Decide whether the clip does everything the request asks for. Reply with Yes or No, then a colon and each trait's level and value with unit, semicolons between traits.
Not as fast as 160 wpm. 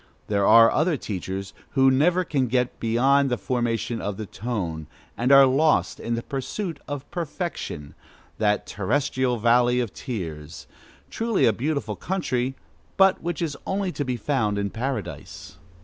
Yes: average, 150 wpm